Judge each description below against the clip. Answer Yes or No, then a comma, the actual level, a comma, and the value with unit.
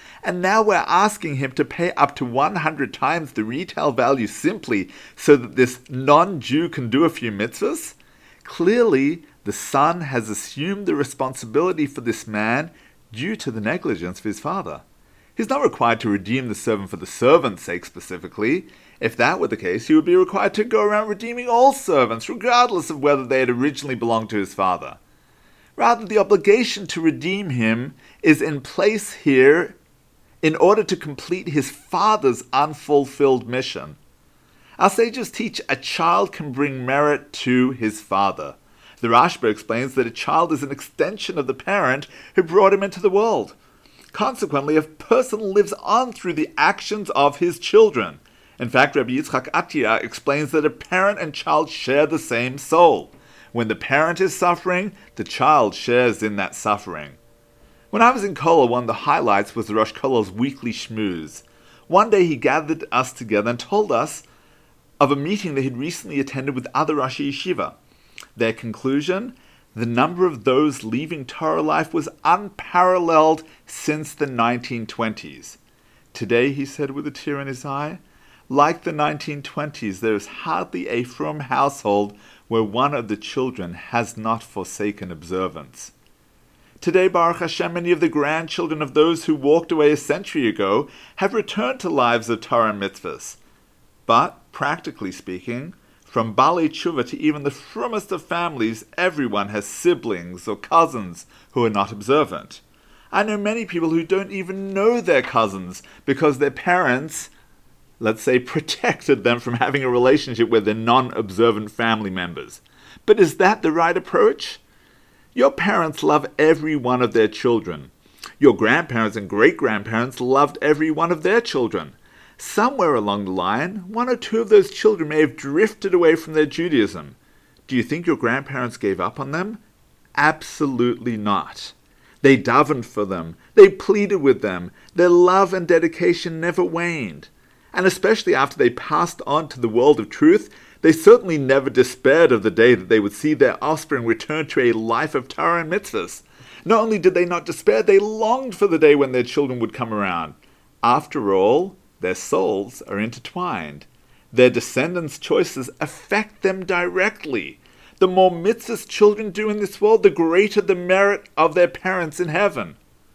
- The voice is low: No, medium, 150 Hz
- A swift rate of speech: No, average, 165 wpm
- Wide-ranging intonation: Yes, wide, 7.7 semitones